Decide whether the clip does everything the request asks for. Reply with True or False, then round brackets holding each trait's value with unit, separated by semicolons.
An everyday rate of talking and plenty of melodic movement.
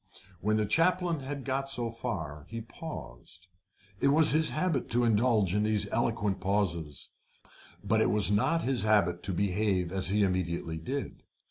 True (160 wpm; 6.2 semitones)